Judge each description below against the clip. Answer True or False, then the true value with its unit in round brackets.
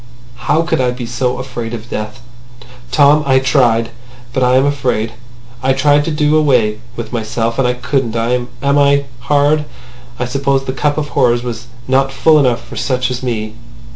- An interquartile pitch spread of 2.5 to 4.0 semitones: True (2.8 semitones)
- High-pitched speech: False (130 Hz)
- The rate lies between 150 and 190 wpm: True (180 wpm)